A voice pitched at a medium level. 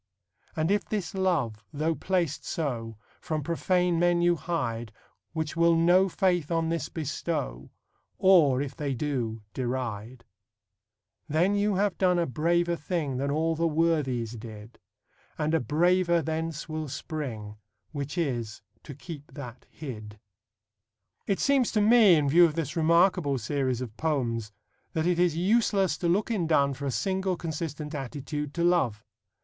Yes: medium, 155 Hz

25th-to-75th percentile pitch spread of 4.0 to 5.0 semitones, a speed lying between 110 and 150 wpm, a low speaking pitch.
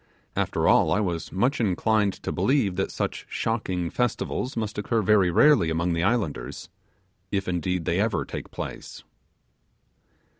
Yes: average, 4.3 semitones; average, 145 wpm; low, 100 Hz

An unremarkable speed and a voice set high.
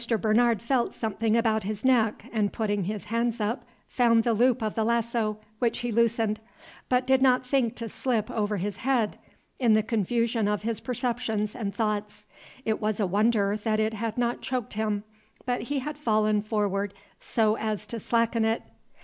Yes: average, 180 wpm; high, 225 Hz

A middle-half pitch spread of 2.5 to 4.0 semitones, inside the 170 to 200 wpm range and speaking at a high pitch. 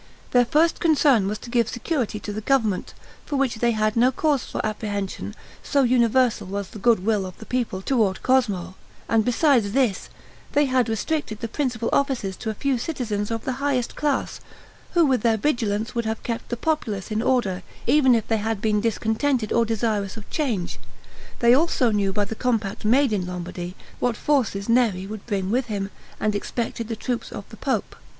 Yes: average, 3.7 semitones; average, 190 wpm; high, 230 Hz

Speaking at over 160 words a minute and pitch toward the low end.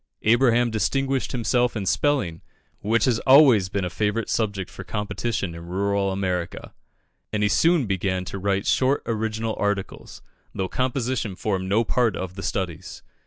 No: average, 155 wpm; low, 105 Hz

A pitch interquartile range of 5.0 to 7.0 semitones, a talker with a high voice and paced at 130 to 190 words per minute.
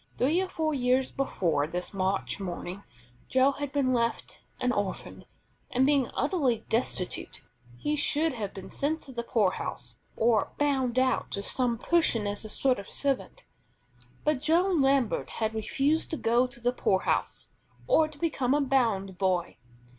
Yes: wide, 5.6 semitones; very high, 250 Hz; average, 160 wpm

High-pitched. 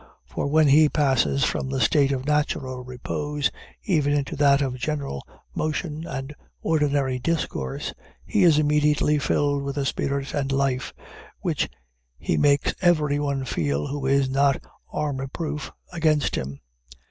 No: medium, 140 Hz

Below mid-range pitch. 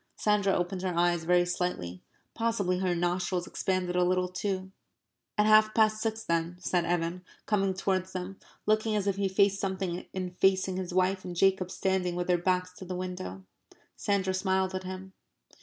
No: medium, 185 Hz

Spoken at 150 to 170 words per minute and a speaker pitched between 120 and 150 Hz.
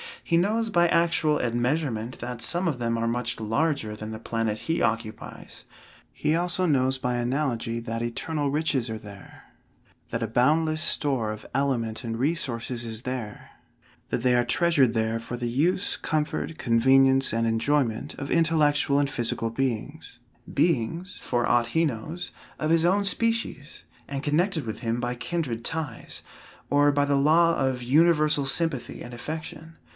Yes: average, 160 wpm; low, 135 Hz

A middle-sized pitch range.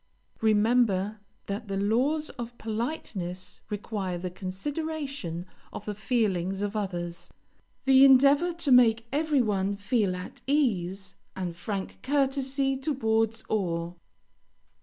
No: wide, 5.9 semitones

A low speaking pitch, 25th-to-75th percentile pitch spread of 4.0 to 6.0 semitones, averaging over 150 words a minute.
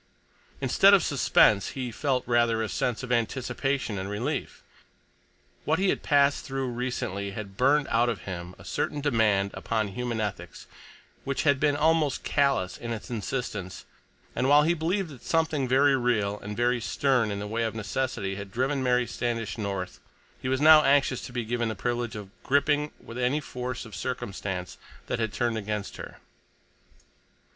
Yes: low, 120 Hz; average, 4.6 semitones; average, 170 wpm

